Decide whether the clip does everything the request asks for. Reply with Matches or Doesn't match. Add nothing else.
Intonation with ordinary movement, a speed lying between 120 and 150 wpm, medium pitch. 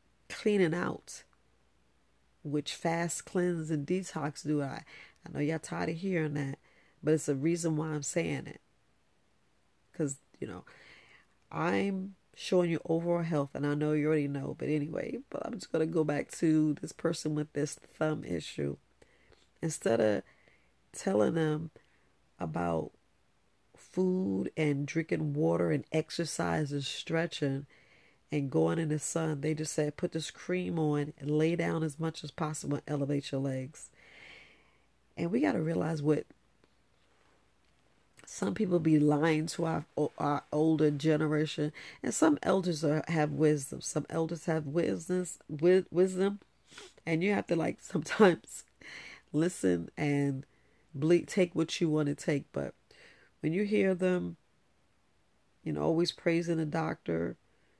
Doesn't match